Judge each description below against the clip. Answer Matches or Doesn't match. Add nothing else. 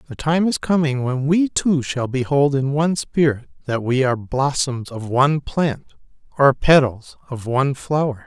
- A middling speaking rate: Matches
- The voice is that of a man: Matches